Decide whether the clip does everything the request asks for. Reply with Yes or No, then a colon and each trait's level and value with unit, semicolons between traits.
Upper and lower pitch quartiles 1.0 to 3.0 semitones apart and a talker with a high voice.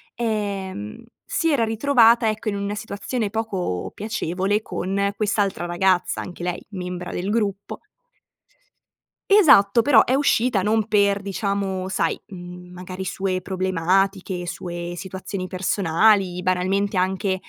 Yes: narrow, 2.6 semitones; high, 195 Hz